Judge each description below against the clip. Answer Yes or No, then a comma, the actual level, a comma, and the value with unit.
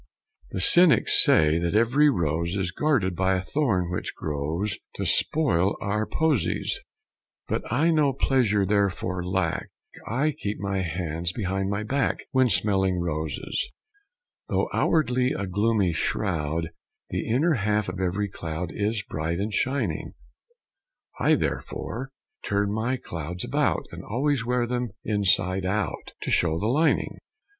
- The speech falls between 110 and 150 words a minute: Yes, average, 140 wpm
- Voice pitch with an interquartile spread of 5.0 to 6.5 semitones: Yes, wide, 5.6 semitones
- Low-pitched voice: Yes, low, 100 Hz